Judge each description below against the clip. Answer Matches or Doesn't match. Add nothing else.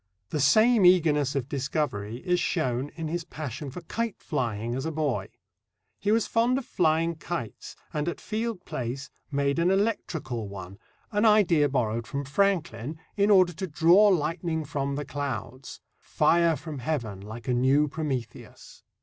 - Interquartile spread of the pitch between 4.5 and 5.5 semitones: Matches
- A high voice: Doesn't match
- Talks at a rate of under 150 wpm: Doesn't match